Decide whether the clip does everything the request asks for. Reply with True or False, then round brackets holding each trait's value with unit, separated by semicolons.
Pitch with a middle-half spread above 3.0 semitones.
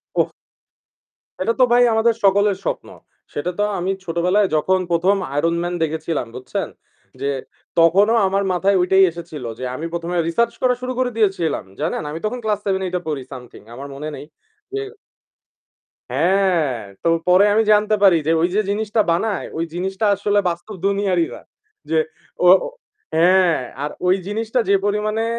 True (3.8 semitones)